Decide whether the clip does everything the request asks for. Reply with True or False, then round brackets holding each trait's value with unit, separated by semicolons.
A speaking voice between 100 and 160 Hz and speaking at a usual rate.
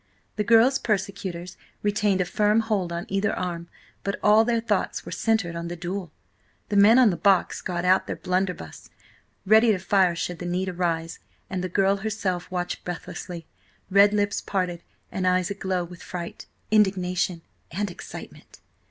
False (185 Hz; 165 wpm)